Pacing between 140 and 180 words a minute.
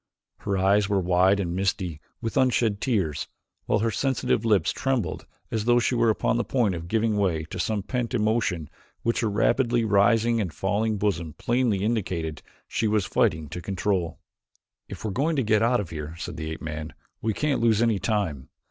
No: average, 195 wpm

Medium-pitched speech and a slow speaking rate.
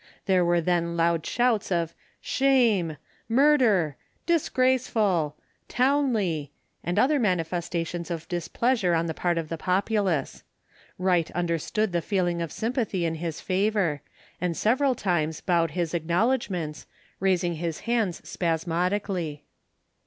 Yes: medium, 180 Hz; slow, 120 wpm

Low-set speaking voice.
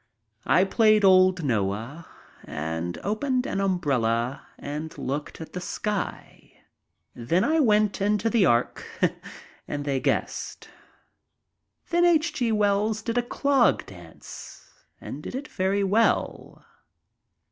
No: high, 190 Hz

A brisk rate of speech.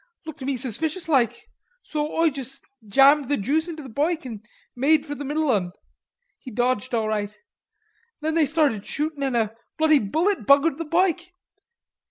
No: average, 165 wpm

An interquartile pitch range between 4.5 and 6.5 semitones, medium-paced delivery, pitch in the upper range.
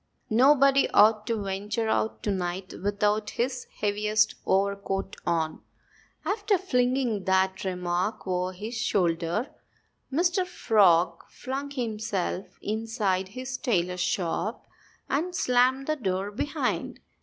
No: average, 5.1 semitones; slow, 115 wpm; high, 210 Hz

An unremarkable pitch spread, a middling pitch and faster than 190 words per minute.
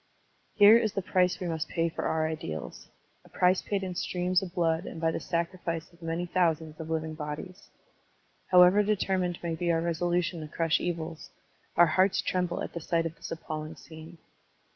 No: narrow, 2.0 semitones; medium, 170 Hz; average, 200 wpm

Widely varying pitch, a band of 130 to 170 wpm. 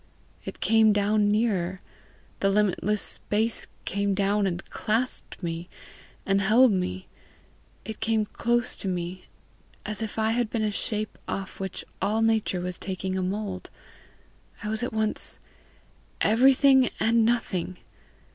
No: average, 2.7 semitones; slow, 135 wpm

